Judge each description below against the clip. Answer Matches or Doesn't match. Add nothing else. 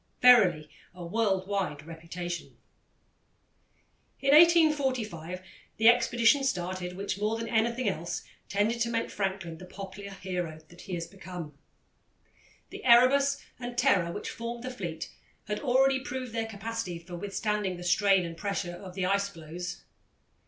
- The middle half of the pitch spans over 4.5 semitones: Matches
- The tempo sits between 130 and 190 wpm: Matches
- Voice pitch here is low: Doesn't match